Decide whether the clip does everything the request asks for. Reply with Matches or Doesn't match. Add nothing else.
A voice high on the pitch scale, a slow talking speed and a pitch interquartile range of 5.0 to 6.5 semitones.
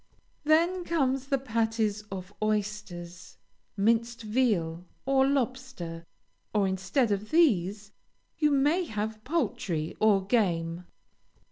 Matches